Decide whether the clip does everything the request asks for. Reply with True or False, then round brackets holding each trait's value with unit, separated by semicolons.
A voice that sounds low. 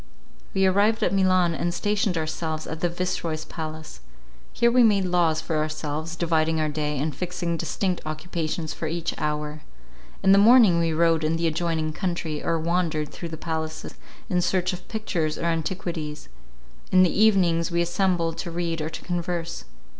False (170 Hz)